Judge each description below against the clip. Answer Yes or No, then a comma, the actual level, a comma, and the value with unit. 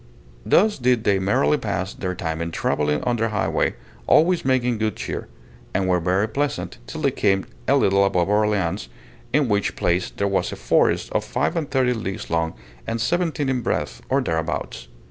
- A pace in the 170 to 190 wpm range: Yes, average, 185 wpm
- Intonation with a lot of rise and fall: Yes, wide, 6.0 semitones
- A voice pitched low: Yes, low, 100 Hz